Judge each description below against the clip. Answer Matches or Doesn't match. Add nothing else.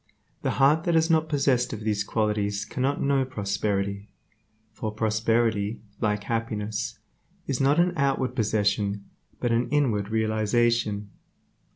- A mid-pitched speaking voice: Doesn't match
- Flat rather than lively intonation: Doesn't match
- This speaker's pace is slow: Matches